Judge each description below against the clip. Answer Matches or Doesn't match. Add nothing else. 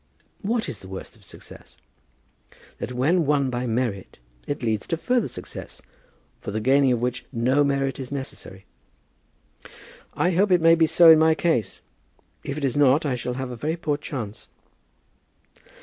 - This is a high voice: Doesn't match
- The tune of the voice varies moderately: Matches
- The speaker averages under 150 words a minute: Doesn't match